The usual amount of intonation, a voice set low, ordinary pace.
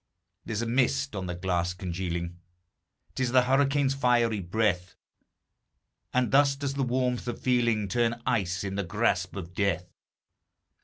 No: wide, 5.7 semitones; low, 115 Hz; average, 150 wpm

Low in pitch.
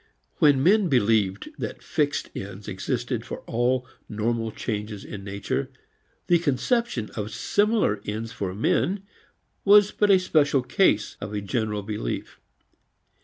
Yes: low, 115 Hz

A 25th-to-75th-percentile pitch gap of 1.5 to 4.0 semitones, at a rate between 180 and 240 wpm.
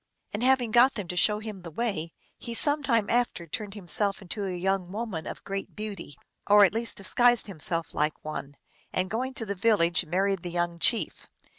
No: average, 4.5 semitones; average, 195 wpm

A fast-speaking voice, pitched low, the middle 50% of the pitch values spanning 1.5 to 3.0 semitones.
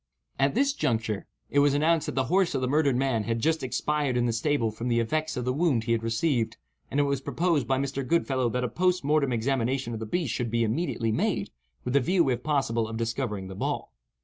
No: fast, 235 wpm; low, 130 Hz; average, 4.4 semitones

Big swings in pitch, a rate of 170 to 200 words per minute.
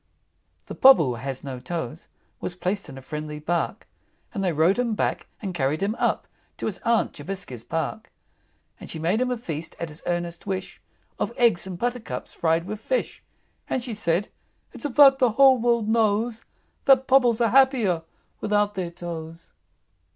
Yes: wide, 6.3 semitones; average, 180 wpm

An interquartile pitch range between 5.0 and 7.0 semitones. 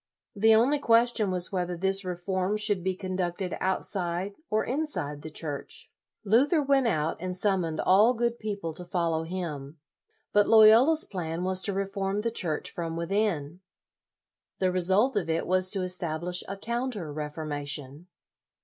No: average, 4.0 semitones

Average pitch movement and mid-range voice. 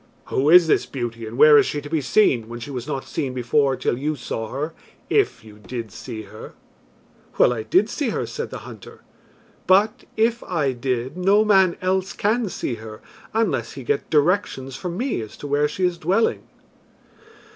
No: wide, 7.5 semitones; medium, 145 Hz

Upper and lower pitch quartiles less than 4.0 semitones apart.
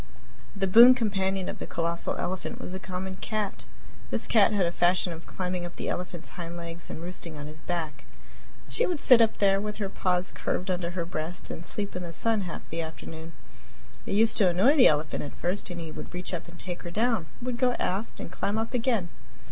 Yes: average, 3.4 semitones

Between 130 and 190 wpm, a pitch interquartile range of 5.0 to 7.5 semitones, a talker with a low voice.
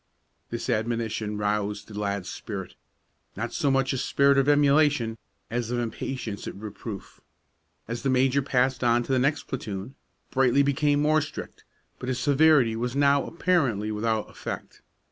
No: average, 155 wpm; average, 4.1 semitones; low, 125 Hz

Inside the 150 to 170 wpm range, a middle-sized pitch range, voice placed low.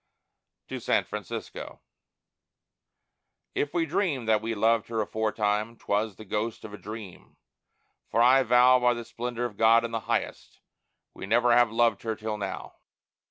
No: average, 160 wpm; narrow, 2.1 semitones; low, 115 Hz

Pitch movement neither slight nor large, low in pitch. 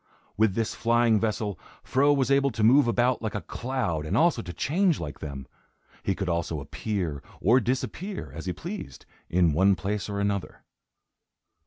No: wide, 6.3 semitones; low, 105 Hz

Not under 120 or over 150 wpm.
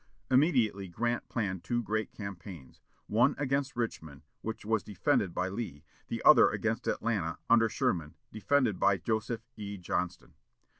Yes: average, 140 wpm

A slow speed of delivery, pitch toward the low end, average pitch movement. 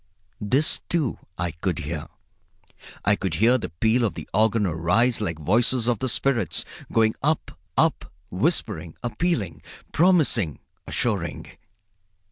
No: slow, 125 wpm; low, 110 Hz; wide, 6.5 semitones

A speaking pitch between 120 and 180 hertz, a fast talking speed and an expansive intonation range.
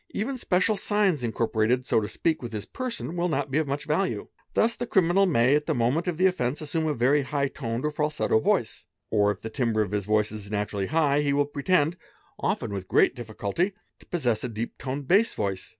Yes: medium, 140 Hz; fast, 225 wpm; wide, 7.4 semitones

